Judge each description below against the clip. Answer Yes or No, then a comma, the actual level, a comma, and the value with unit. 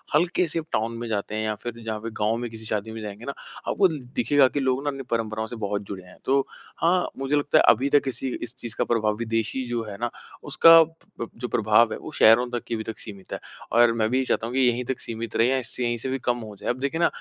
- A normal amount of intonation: Yes, average, 3.2 semitones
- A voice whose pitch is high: No, low, 120 Hz